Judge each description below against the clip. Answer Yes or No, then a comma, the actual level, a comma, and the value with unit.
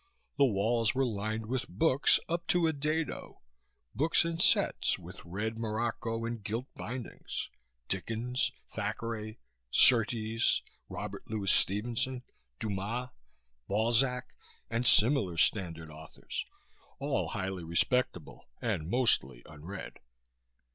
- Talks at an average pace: No, slow, 105 wpm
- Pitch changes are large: No, average, 4.0 semitones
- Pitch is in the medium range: No, low, 115 Hz